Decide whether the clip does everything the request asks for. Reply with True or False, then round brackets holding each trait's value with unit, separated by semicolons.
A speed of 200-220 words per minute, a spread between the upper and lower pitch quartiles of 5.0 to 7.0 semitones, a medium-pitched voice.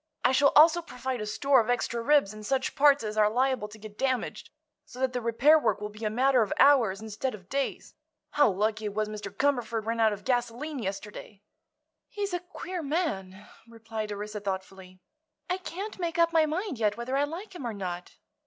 False (205 wpm; 5.3 semitones; 235 Hz)